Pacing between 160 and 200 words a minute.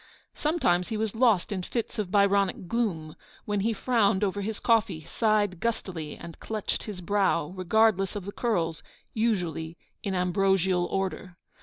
No: average, 150 wpm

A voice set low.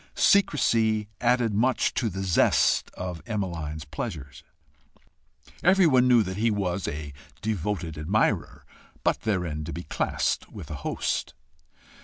Yes: low, 100 Hz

